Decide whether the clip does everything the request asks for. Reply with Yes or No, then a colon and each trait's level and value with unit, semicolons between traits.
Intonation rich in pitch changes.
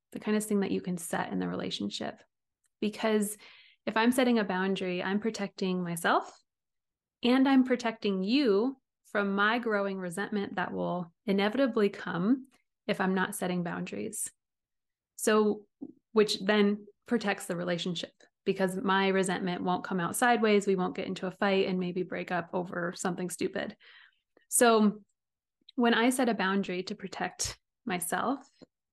No: average, 3.3 semitones